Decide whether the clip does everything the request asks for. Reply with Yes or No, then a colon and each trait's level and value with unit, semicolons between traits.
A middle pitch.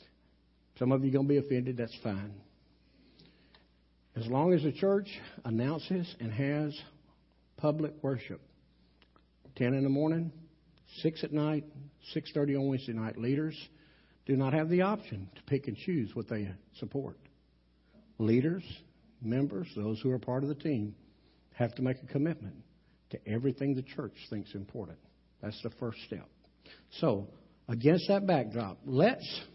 No: low, 130 Hz